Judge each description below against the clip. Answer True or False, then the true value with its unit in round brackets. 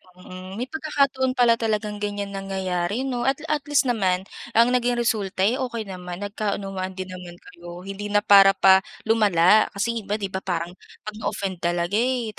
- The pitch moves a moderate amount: True (3.8 semitones)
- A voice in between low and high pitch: False (205 Hz)